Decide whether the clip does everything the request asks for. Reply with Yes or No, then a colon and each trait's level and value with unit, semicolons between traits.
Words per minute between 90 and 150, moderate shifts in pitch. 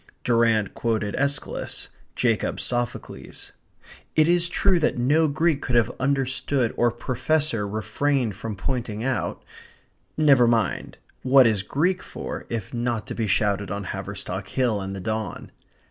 Yes: average, 140 wpm; average, 4.7 semitones